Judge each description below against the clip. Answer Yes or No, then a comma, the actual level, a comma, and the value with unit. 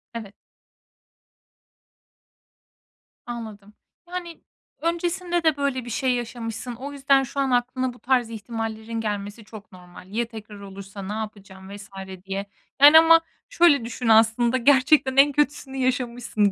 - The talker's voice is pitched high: Yes, high, 240 Hz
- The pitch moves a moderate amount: Yes, average, 4.3 semitones